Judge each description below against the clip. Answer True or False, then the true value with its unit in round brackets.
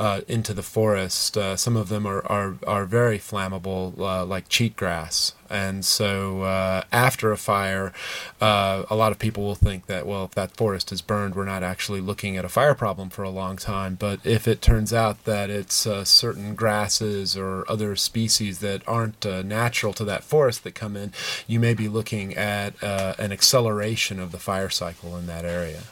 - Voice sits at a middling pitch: False (100 Hz)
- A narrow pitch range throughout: True (2.3 semitones)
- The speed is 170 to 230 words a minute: True (200 wpm)